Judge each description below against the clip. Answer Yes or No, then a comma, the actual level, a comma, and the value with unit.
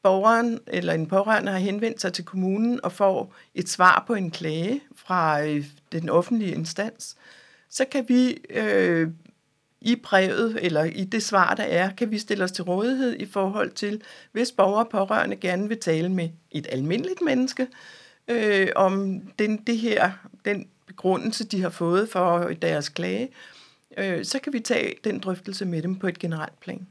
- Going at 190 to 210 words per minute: No, average, 175 wpm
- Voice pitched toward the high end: Yes, high, 195 Hz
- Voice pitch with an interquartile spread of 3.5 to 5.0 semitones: Yes, average, 4.2 semitones